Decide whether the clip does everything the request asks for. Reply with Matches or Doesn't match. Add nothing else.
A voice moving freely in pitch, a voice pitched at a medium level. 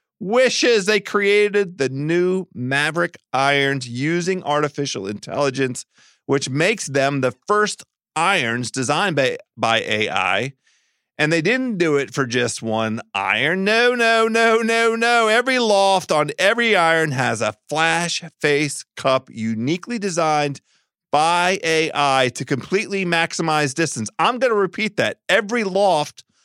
Matches